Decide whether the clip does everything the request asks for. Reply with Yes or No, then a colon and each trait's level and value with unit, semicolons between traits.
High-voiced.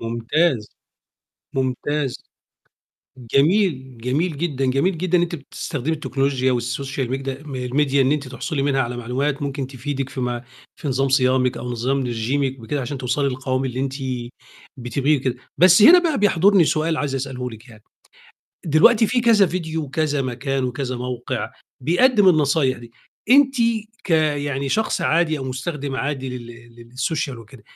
No: low, 135 Hz